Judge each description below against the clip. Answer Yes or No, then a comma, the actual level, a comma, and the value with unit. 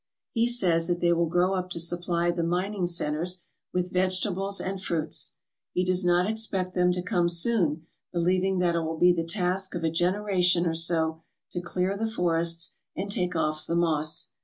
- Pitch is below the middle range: No, medium, 175 Hz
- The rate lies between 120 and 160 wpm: No, average, 190 wpm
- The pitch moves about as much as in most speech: No, narrow, 1.8 semitones